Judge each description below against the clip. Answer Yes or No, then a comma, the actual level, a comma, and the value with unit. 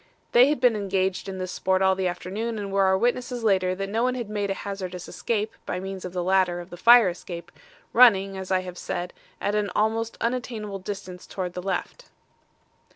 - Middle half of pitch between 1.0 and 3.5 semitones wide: Yes, average, 3.2 semitones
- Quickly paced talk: Yes, fast, 210 wpm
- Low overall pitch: No, high, 195 Hz